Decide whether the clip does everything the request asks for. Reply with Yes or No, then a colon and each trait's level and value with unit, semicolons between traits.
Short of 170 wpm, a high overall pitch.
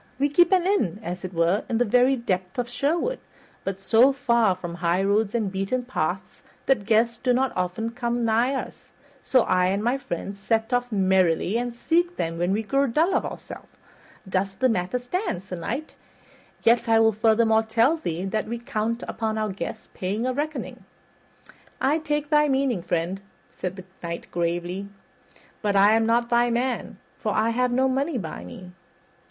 No: average, 180 wpm; high, 225 Hz